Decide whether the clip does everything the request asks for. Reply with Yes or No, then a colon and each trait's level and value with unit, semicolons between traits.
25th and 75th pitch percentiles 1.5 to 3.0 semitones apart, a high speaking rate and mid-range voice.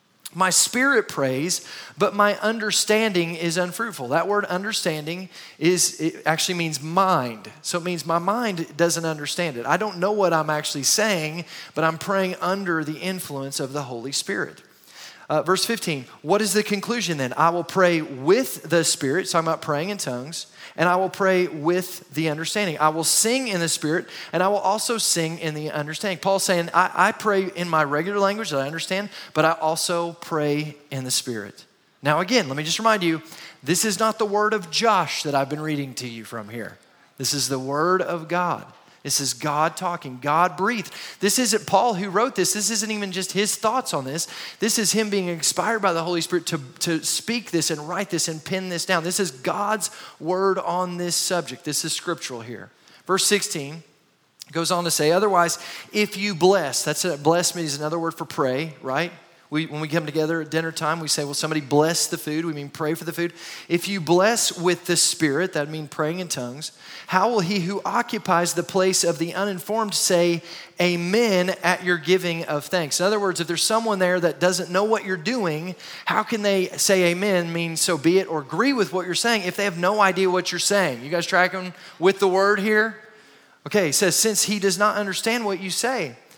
No: average, 3.7 semitones; fast, 210 wpm; medium, 175 Hz